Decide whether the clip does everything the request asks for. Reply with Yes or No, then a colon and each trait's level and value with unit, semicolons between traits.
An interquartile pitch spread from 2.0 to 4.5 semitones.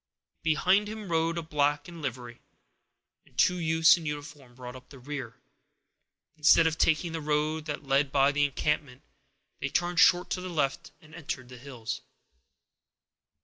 Yes: average, 3.1 semitones